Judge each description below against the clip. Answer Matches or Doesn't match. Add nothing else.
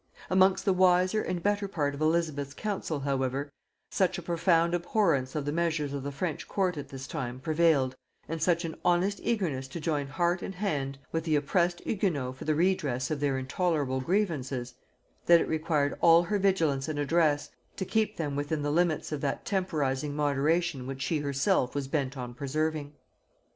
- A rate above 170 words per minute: Matches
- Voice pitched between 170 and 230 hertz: Doesn't match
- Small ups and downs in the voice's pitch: Doesn't match